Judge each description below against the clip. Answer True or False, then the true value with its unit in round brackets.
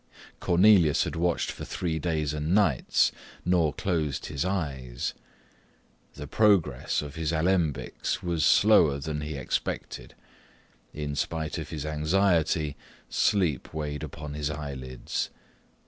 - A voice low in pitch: True (75 Hz)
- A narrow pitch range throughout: False (3.1 semitones)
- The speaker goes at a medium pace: False (120 wpm)